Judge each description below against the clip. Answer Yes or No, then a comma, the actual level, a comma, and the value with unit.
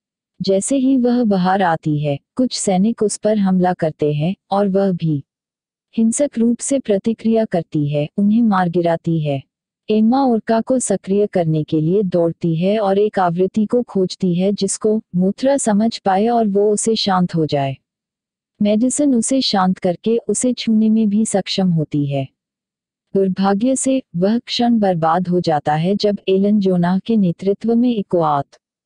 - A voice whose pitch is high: Yes, high, 200 Hz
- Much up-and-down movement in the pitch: No, average, 3.8 semitones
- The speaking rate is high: No, average, 160 wpm